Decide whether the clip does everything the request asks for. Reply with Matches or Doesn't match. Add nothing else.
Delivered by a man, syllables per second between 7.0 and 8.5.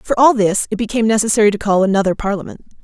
Doesn't match